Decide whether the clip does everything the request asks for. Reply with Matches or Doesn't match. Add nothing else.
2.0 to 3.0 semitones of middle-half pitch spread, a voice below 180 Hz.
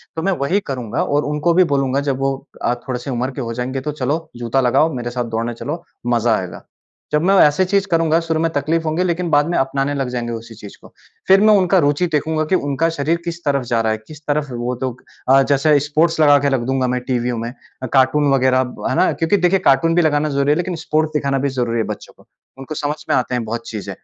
Doesn't match